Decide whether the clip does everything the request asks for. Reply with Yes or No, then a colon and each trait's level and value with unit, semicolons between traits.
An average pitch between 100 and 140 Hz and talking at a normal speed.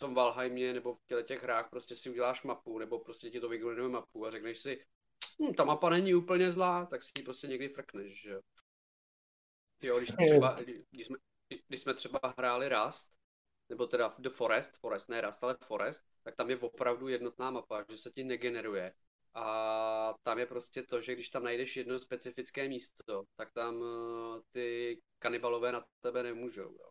No: low, 125 Hz; fast, 185 wpm